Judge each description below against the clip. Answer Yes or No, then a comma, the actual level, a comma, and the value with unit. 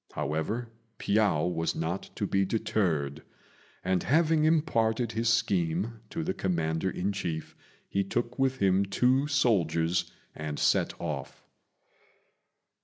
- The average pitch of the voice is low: Yes, low, 100 Hz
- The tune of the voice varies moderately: No, wide, 6.2 semitones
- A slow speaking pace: Yes, slow, 120 wpm